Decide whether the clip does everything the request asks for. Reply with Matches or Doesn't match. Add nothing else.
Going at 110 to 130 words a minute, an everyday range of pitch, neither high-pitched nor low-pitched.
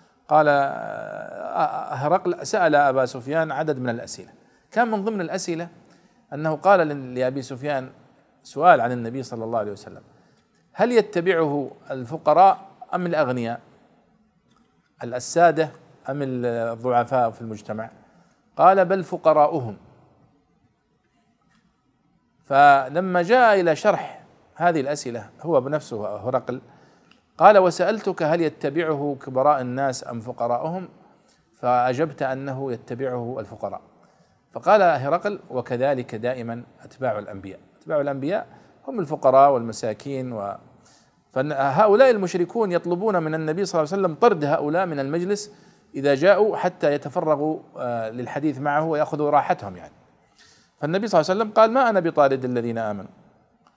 Doesn't match